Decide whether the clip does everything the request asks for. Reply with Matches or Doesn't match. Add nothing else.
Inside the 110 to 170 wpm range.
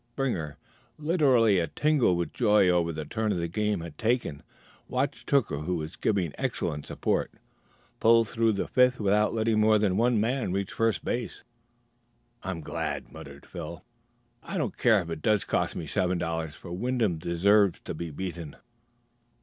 Matches